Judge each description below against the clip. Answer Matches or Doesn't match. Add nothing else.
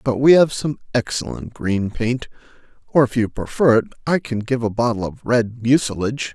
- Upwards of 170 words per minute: Matches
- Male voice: Matches